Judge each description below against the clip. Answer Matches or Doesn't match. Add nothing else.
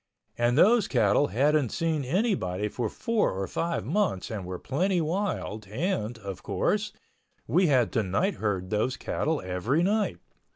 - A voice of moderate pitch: Doesn't match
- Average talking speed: Matches